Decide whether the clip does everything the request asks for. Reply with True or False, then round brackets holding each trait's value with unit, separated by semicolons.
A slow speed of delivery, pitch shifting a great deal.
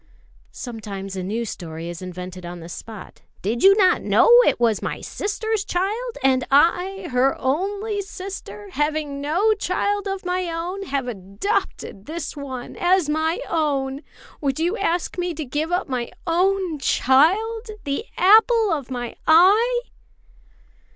False (150 wpm; 7.6 semitones)